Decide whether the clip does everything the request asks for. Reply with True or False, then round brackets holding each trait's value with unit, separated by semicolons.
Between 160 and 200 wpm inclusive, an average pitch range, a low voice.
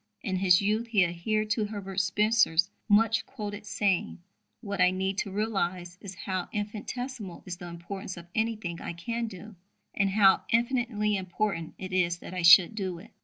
False (170 wpm; 3.0 semitones; 195 Hz)